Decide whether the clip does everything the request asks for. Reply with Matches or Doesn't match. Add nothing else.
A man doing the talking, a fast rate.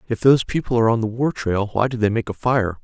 Matches